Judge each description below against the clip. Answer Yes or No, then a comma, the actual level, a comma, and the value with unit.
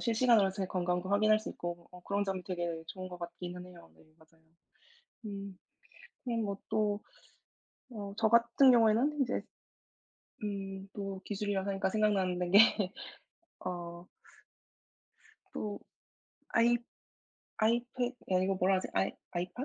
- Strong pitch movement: No, average, 3.2 semitones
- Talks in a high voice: Yes, high, 195 Hz